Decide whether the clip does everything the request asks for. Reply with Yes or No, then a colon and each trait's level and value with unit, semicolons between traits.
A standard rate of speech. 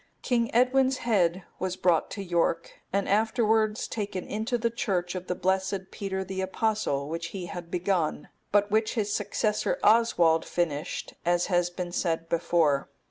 Yes: average, 155 wpm